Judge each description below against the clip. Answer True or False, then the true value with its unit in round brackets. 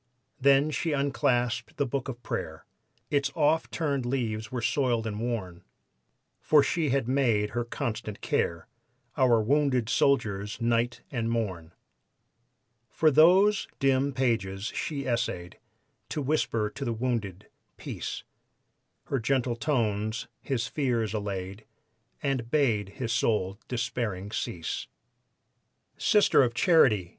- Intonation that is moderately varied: True (4.3 semitones)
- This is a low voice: True (120 Hz)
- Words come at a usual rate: False (120 wpm)